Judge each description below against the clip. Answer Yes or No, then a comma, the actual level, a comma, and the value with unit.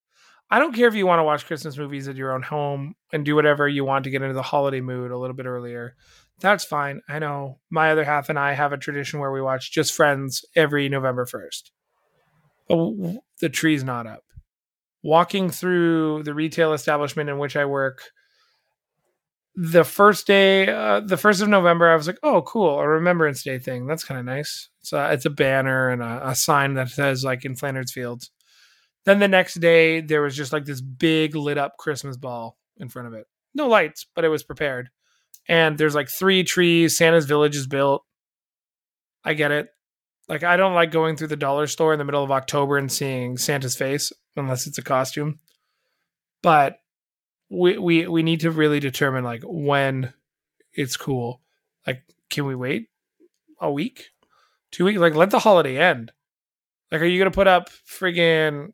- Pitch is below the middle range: No, medium, 150 Hz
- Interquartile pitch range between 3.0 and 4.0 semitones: Yes, average, 3.6 semitones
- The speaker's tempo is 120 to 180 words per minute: No, average, 195 wpm